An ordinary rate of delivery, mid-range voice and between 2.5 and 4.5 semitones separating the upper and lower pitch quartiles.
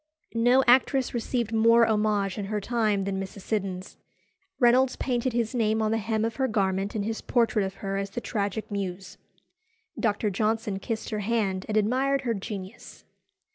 No: average, 175 wpm; high, 215 Hz; average, 2.9 semitones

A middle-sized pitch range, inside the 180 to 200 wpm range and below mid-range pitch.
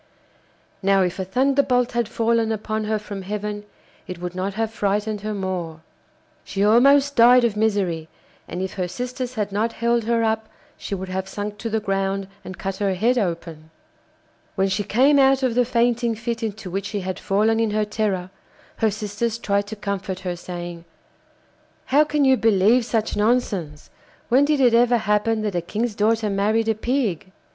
No: average, 3.2 semitones; average, 185 wpm; high, 210 Hz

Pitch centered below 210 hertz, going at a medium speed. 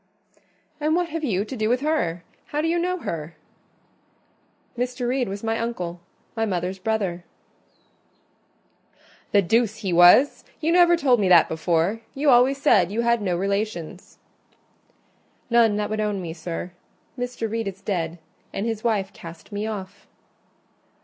No: high, 215 Hz; average, 150 wpm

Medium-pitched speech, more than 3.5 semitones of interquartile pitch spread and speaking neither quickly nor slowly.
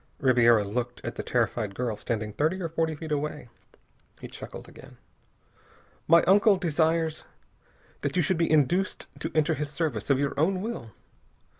Yes: medium, 150 Hz; wide, 5.4 semitones; average, 160 wpm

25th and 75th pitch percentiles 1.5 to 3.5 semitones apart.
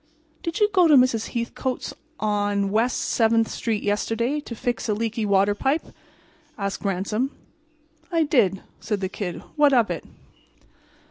No: average, 4.1 semitones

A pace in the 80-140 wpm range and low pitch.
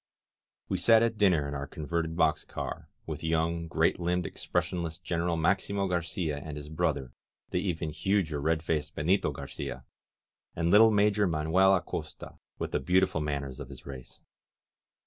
No: average, 160 wpm; very low, 85 Hz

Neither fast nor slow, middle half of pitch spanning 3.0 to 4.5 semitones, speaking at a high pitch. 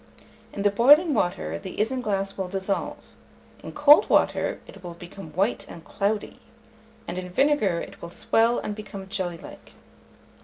Yes: average, 155 wpm; average, 3.8 semitones; high, 200 Hz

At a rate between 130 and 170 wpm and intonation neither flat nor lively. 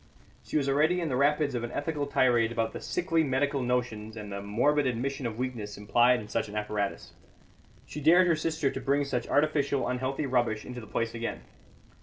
No: average, 200 wpm; average, 4.0 semitones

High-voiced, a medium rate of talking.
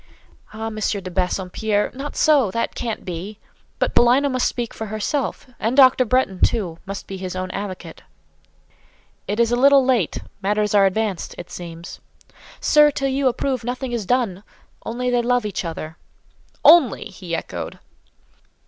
Yes: high, 220 Hz; average, 150 wpm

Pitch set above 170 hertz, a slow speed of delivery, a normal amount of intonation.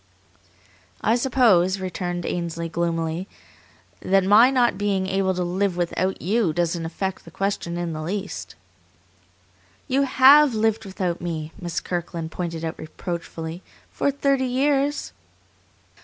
Yes: medium, 185 Hz; slow, 125 wpm; average, 4.6 semitones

